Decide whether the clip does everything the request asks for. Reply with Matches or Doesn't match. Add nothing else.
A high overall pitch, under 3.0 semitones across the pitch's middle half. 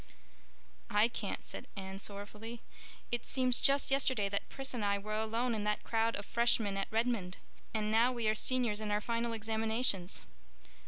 Matches